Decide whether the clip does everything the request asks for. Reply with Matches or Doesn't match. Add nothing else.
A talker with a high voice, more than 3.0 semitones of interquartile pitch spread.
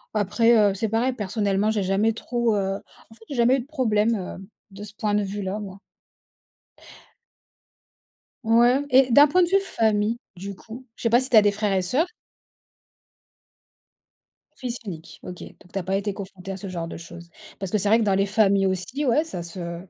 Matches